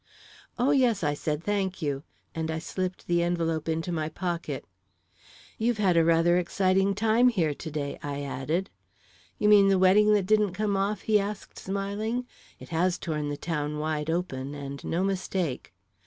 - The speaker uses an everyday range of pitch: Yes, average, 4.1 semitones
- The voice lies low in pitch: No, medium, 180 Hz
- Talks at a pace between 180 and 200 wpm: No, average, 170 wpm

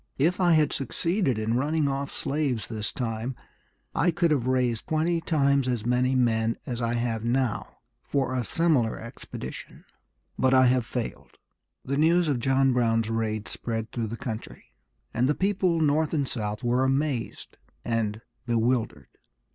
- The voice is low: Yes, low, 130 Hz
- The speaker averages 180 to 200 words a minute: No, average, 155 wpm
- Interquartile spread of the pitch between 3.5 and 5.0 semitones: Yes, average, 4.2 semitones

